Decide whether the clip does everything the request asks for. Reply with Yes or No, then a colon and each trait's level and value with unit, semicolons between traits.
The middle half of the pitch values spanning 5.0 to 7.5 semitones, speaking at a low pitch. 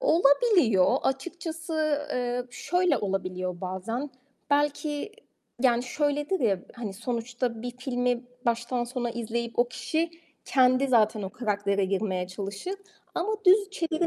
No: average, 5.3 semitones; high, 245 Hz